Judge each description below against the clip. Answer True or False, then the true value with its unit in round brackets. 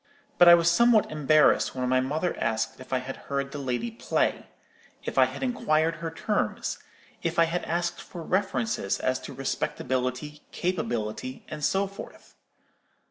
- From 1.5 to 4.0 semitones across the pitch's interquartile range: False (5.0 semitones)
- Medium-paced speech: True (160 wpm)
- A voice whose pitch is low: False (155 Hz)